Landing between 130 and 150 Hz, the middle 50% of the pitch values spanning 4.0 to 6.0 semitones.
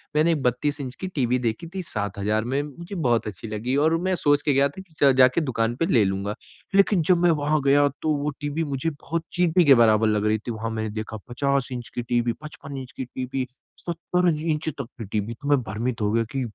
Yes: low, 135 Hz; average, 5.1 semitones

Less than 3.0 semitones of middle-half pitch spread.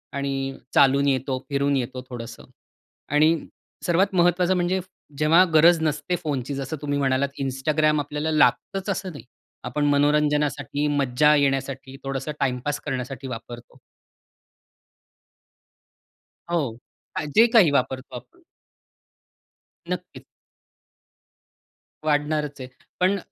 Yes: narrow, 2.5 semitones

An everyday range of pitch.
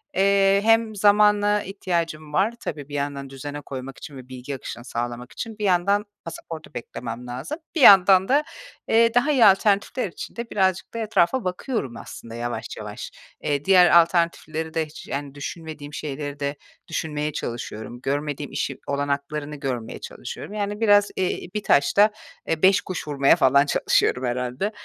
No: wide, 6.4 semitones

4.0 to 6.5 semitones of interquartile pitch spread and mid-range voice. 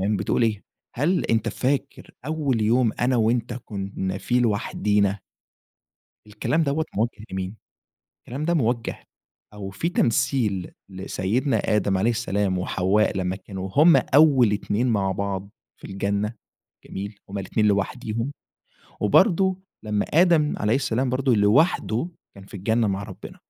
No: average, 4.4 semitones; low, 110 Hz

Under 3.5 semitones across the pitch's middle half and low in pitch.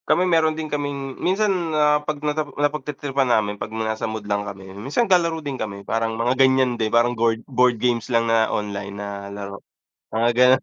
No: average, 5.0 semitones; low, 120 Hz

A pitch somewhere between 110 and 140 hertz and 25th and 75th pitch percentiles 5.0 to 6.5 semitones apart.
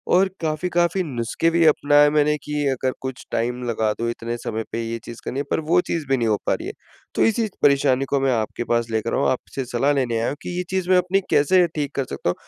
Yes: low, 135 Hz; wide, 5.5 semitones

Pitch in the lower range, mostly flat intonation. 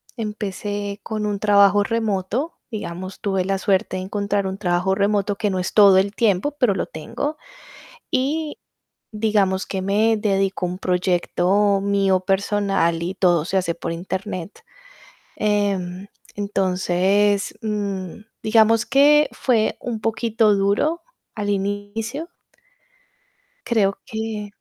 No: high, 200 Hz; narrow, 2.3 semitones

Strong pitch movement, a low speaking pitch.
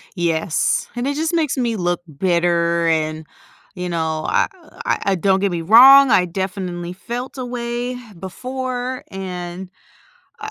No: wide, 6.2 semitones; high, 190 Hz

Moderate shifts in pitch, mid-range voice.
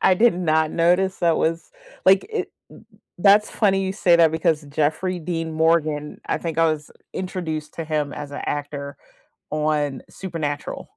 Yes: average, 3.2 semitones; medium, 160 Hz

